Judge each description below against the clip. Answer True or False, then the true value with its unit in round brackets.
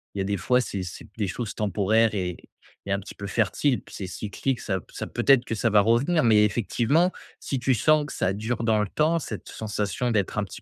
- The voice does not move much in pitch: False (3.6 semitones)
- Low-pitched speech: True (110 Hz)